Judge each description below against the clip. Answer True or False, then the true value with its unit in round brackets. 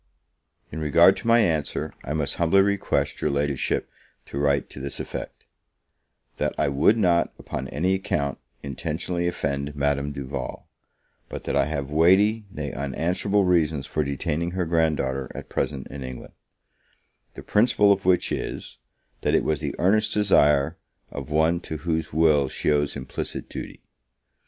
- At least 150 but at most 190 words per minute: True (155 wpm)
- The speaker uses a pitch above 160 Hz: False (75 Hz)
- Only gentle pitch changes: False (4.1 semitones)